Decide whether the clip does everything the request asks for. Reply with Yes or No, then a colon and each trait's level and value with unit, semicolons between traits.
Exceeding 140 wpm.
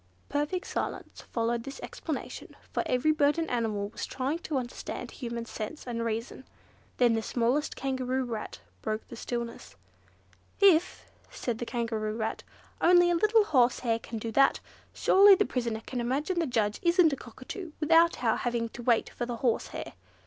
Yes: average, 165 wpm